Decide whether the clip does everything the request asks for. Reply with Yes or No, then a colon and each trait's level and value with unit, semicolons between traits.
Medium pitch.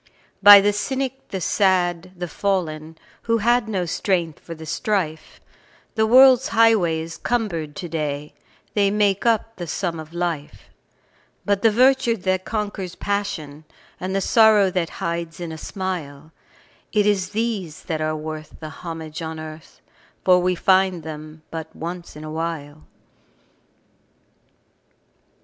Yes: medium, 180 Hz